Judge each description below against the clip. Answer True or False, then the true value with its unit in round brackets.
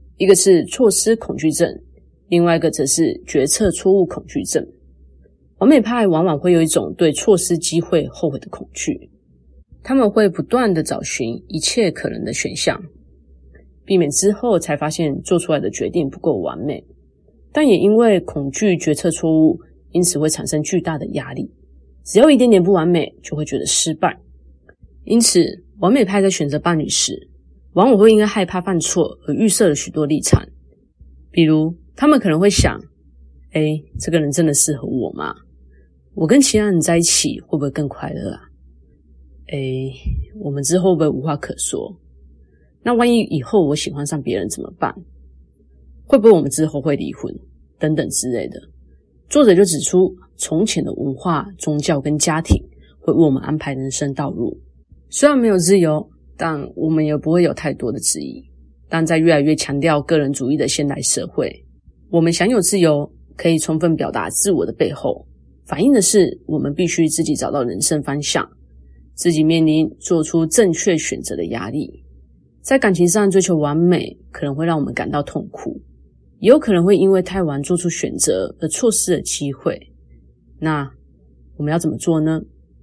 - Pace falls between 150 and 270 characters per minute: True (260 characters per minute)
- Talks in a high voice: False (155 Hz)